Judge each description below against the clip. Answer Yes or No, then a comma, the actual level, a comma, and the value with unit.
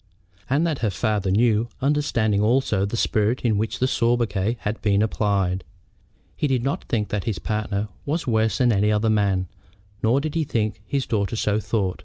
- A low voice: Yes, low, 110 Hz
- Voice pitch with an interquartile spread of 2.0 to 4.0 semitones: Yes, average, 3.0 semitones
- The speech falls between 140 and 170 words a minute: No, average, 185 wpm